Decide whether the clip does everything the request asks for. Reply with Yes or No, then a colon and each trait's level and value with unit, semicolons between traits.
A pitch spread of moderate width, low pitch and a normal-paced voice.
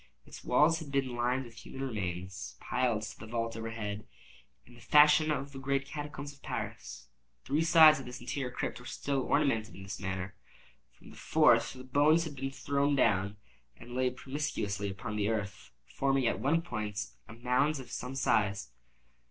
Yes: average, 4.6 semitones; low, 125 Hz; average, 180 wpm